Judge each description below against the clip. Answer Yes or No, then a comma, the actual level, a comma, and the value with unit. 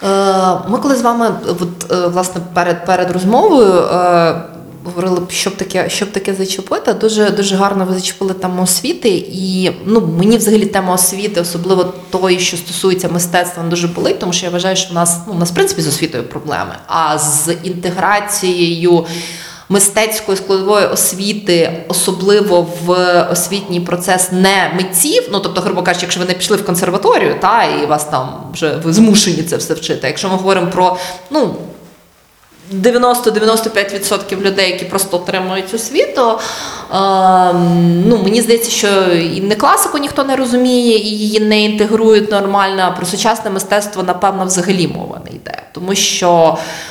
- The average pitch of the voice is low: No, medium, 185 Hz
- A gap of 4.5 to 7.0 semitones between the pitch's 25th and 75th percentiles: No, narrow, 2.5 semitones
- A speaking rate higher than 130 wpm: Yes, fast, 155 wpm